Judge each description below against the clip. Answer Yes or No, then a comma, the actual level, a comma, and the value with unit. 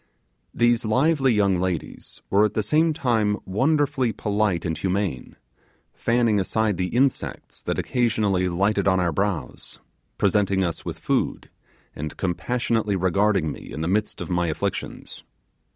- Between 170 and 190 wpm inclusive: No, average, 140 wpm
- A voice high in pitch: No, low, 105 Hz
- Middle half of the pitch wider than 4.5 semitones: No, average, 4.1 semitones